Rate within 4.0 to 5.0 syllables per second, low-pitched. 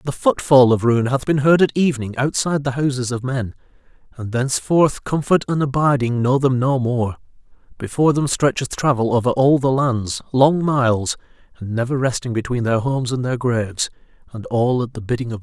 No: 5.5 syllables/s; low, 130 Hz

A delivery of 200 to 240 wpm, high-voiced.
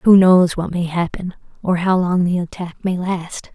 No: fast, 205 wpm; medium, 180 Hz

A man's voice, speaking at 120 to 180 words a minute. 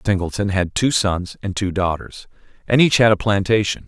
No: male; average, 200 wpm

